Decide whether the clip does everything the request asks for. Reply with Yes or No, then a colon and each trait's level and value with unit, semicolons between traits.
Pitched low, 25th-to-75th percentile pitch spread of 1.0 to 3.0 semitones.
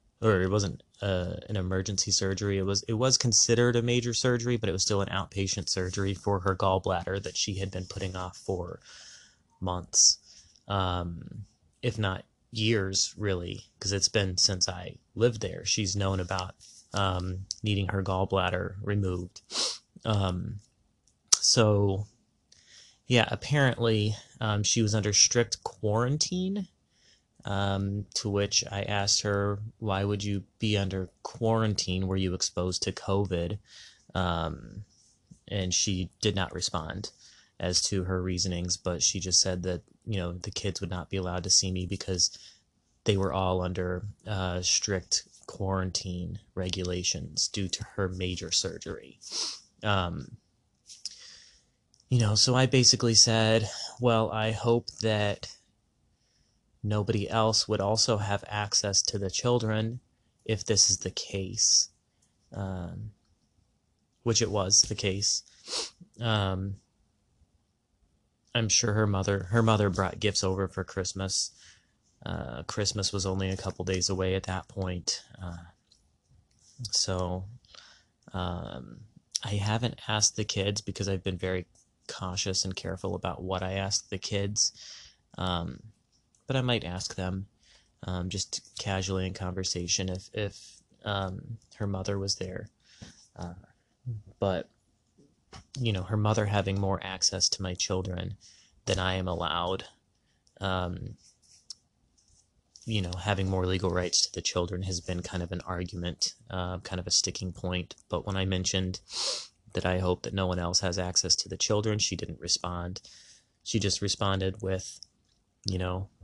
Yes: very low, 95 Hz; average, 2.7 semitones